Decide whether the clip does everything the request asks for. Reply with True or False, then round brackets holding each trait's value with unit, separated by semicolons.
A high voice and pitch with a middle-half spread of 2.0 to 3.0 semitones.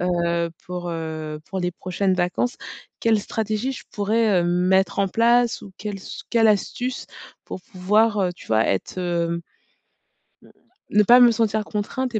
False (195 Hz; 4.0 semitones)